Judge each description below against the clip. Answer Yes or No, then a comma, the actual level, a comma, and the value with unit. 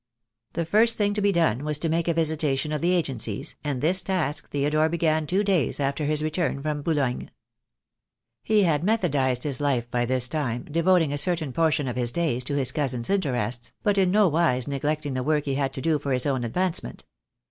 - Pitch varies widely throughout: No, average, 4.1 semitones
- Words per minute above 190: Yes, fast, 205 wpm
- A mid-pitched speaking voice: Yes, medium, 150 Hz